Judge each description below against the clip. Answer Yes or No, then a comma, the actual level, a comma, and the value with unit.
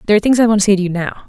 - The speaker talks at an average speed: No, fast, 470 wpm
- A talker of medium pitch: No, high, 205 Hz